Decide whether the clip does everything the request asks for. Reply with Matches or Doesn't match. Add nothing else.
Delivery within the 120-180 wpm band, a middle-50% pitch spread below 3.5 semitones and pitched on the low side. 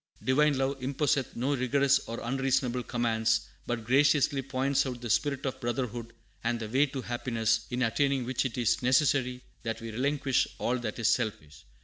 Matches